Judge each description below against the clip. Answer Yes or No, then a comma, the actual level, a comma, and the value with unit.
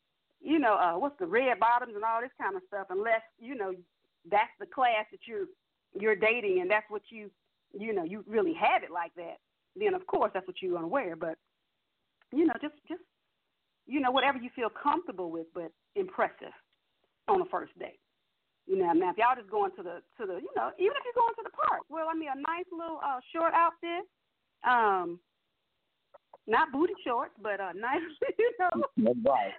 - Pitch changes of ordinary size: No, wide, 8.7 semitones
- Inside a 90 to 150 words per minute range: No, fast, 205 wpm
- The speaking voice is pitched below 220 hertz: No, very high, 270 Hz